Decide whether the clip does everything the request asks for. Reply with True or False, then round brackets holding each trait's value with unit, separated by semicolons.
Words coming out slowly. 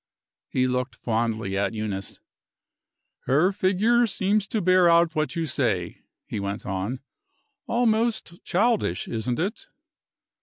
True (120 wpm)